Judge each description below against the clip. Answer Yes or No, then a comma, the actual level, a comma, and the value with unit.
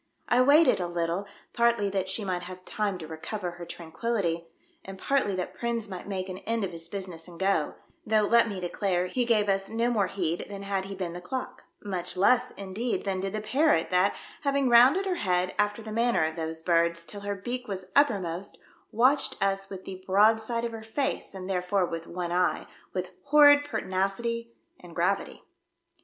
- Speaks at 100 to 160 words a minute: No, average, 200 wpm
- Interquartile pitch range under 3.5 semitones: No, average, 4.3 semitones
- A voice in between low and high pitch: No, high, 195 Hz